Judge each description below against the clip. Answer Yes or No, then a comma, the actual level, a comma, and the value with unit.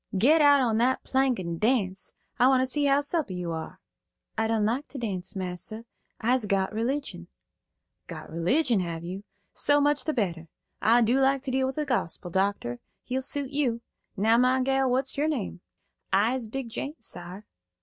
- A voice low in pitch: No, high, 240 Hz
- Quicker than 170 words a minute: Yes, average, 180 wpm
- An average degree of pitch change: No, wide, 5.8 semitones